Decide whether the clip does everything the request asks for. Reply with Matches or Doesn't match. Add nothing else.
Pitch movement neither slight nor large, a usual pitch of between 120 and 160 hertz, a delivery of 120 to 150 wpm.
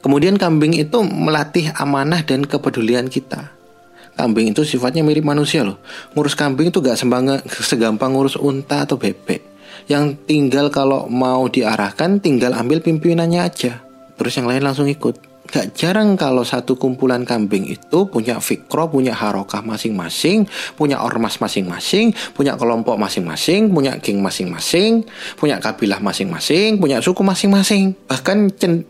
Matches